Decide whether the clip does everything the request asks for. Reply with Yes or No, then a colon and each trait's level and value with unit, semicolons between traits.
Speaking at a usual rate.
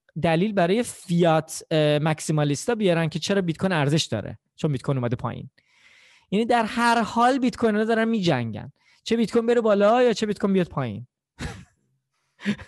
No: fast, 165 wpm